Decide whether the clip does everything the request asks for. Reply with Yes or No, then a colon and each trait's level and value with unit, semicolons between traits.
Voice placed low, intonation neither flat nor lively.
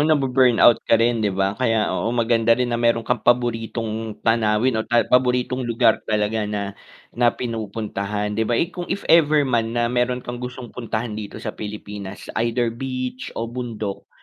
No: low, 115 Hz; narrow, 2.3 semitones